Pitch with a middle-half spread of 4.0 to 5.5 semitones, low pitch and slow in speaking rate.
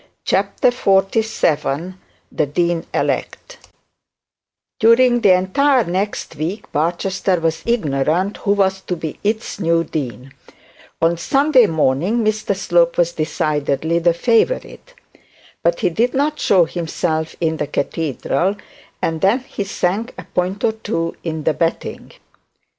No: average, 4.8 semitones; medium, 180 Hz; slow, 130 wpm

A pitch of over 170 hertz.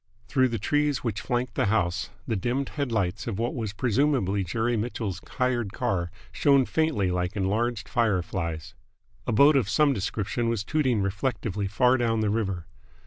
No: low, 115 Hz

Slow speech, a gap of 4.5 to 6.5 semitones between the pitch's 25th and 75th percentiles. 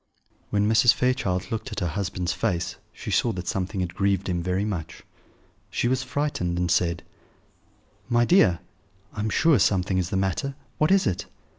No: average, 175 wpm; average, 4.9 semitones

